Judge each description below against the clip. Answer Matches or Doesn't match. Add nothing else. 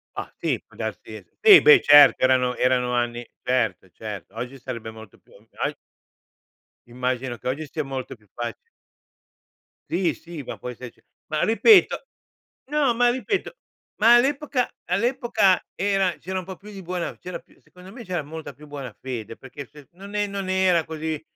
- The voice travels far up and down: Matches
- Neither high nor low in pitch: Matches